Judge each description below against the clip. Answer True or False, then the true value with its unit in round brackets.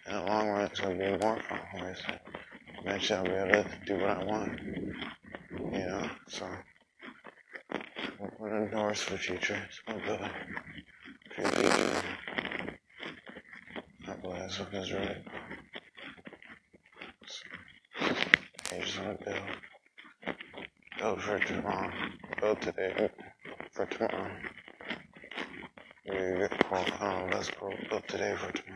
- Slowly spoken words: True (100 wpm)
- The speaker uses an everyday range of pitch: False (1.5 semitones)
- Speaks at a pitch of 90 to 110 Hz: True (100 Hz)